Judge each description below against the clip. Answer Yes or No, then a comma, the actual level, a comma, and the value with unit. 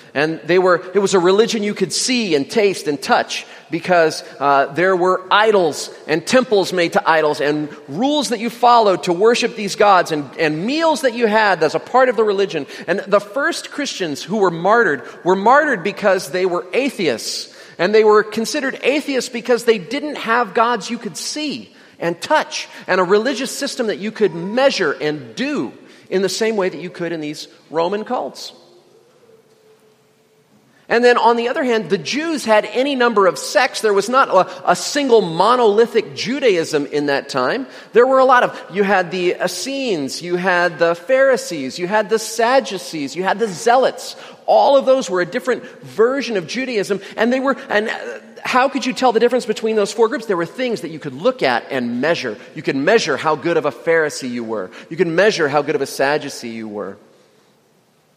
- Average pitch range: No, wide, 6.2 semitones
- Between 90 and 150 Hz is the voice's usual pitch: No, high, 210 Hz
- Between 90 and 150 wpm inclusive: No, average, 195 wpm